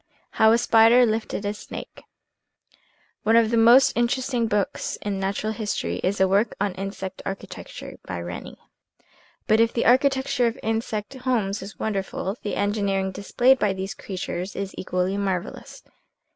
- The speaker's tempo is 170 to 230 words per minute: No, average, 160 wpm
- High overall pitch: Yes, high, 210 Hz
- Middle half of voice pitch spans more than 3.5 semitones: No, average, 3.0 semitones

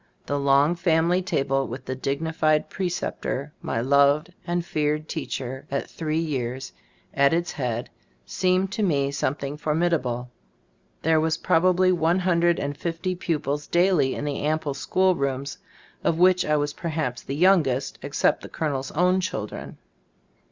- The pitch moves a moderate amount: Yes, average, 3.8 semitones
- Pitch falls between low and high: Yes, medium, 150 Hz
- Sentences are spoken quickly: No, average, 150 wpm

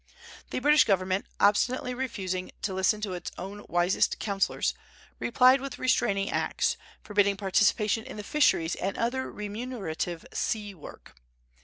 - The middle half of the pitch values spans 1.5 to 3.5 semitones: No, average, 4.1 semitones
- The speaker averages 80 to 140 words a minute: Yes, slow, 135 wpm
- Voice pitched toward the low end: No, high, 205 Hz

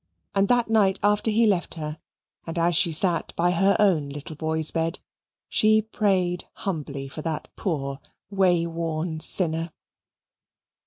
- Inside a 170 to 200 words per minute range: No, average, 145 wpm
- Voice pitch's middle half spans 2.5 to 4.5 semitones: Yes, average, 3.7 semitones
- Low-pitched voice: No, medium, 170 Hz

